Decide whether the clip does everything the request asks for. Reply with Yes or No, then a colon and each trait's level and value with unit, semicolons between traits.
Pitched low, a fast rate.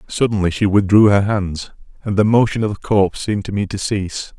Yes: low, 100 Hz; fast, 220 wpm